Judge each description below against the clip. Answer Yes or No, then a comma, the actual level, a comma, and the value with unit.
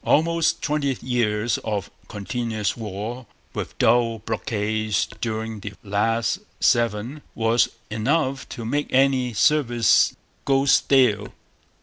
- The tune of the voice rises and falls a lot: No, average, 3.7 semitones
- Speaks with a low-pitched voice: Yes, low, 115 Hz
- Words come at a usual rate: No, slow, 105 wpm